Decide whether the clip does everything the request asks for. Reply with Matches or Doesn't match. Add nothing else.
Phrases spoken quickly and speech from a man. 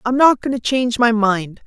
Doesn't match